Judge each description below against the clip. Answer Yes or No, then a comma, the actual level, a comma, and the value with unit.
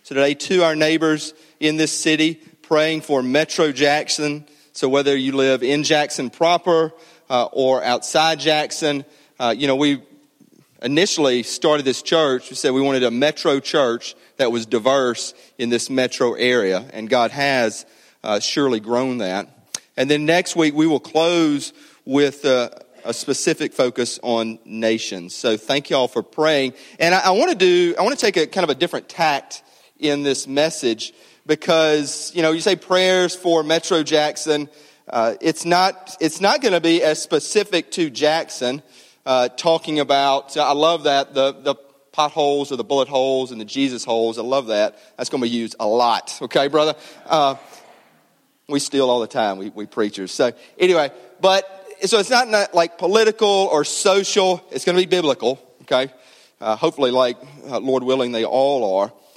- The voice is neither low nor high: Yes, medium, 150 Hz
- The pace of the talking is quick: No, average, 180 wpm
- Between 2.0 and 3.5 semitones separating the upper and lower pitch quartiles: No, average, 4.0 semitones